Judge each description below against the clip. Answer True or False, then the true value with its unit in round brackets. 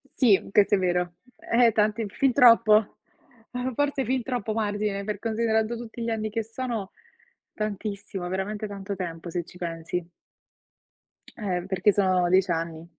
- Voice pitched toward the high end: True (210 Hz)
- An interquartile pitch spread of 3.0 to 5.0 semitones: True (3.5 semitones)